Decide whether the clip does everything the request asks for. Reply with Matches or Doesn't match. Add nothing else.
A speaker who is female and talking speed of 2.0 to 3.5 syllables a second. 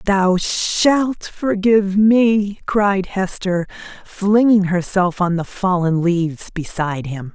Matches